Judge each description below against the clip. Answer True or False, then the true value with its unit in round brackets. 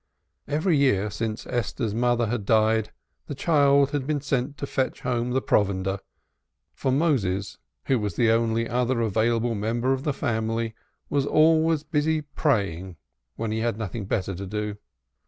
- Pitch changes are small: False (4.6 semitones)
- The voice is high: False (120 Hz)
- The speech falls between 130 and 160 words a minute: True (155 wpm)